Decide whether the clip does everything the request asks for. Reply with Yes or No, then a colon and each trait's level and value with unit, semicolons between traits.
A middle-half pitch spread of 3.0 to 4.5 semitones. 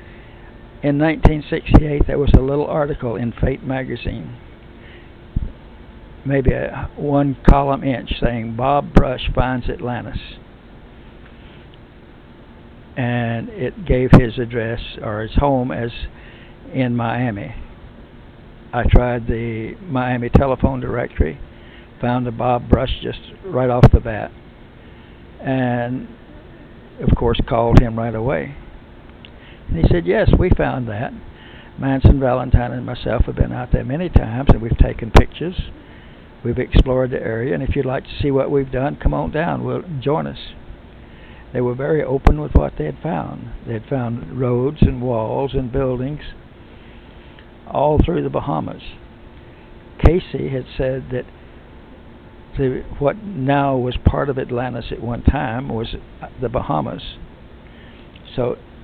No: narrow, 2.6 semitones